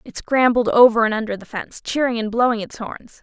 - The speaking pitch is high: Yes, high, 230 Hz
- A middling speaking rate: No, fast, 225 wpm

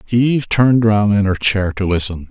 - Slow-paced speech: No, fast, 210 wpm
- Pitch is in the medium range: No, low, 105 Hz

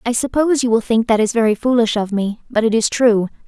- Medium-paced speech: No, fast, 260 wpm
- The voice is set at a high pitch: Yes, high, 230 Hz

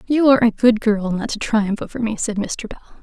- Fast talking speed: Yes, fast, 260 wpm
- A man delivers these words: No, female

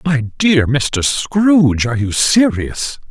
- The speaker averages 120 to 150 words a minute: Yes, slow, 135 wpm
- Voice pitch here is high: No, medium, 145 Hz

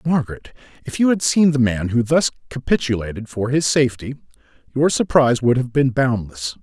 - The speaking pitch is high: No, low, 125 Hz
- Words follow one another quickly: No, average, 170 wpm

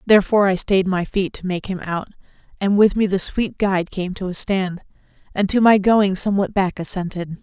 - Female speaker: Yes, female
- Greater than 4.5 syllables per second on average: Yes, 5.4 syllables/s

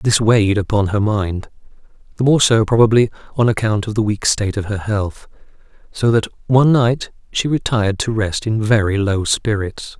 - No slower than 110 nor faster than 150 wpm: No, average, 180 wpm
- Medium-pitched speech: No, low, 110 Hz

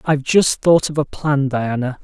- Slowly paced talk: No, fast, 205 wpm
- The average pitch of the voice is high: No, medium, 140 Hz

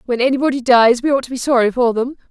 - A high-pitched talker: Yes, very high, 250 Hz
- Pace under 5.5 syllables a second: No, 6.8 syllables/s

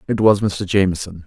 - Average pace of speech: Yes, average, 190 wpm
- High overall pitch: No, very low, 95 Hz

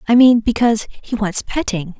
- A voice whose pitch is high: Yes, high, 220 Hz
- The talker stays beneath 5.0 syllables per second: No, 5.1 syllables/s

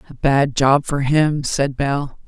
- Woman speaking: Yes, female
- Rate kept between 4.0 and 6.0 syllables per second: No, 3.5 syllables/s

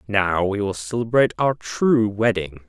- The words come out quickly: No, average, 155 wpm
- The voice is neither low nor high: No, low, 105 Hz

